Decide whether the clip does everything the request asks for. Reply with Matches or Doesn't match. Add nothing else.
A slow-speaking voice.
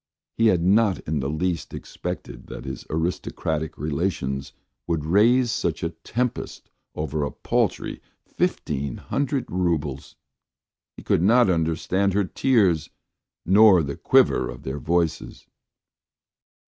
Matches